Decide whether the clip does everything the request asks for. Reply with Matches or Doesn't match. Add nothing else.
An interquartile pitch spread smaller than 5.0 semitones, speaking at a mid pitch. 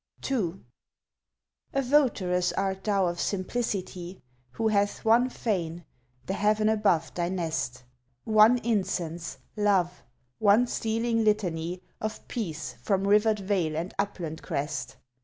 Doesn't match